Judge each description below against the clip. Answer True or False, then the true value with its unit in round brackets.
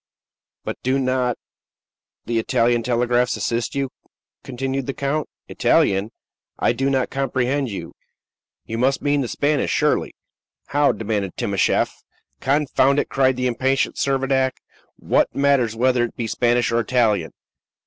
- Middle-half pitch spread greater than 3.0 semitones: False (2.4 semitones)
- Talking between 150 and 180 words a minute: False (135 wpm)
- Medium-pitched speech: False (130 Hz)